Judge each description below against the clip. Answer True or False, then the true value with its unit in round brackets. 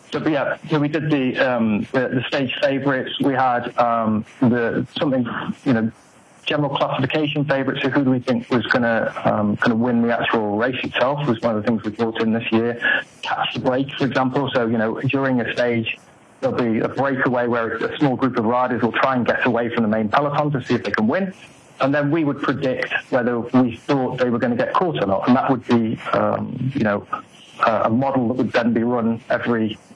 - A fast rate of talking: True (225 wpm)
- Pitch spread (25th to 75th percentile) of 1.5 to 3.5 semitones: True (3.1 semitones)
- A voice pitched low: True (125 Hz)